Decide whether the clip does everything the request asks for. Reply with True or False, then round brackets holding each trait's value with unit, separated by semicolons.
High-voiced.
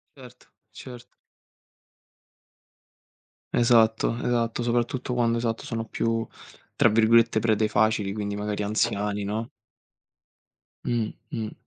False (115 Hz)